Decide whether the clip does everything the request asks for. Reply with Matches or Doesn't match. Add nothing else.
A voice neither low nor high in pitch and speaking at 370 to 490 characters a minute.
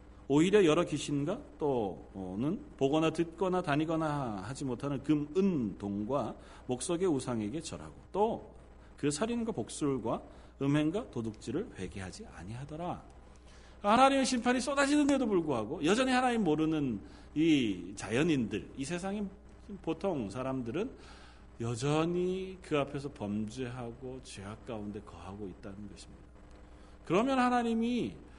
Doesn't match